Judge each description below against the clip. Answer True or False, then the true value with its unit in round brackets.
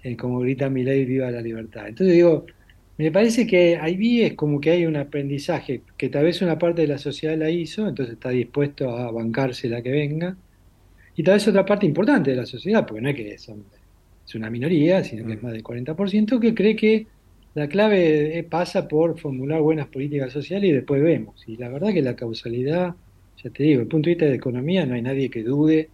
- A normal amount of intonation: False (5.7 semitones)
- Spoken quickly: True (225 wpm)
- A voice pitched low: False (145 Hz)